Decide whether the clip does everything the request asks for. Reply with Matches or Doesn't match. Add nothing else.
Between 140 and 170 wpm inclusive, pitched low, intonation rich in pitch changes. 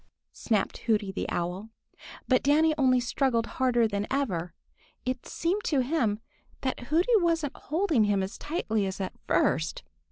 Doesn't match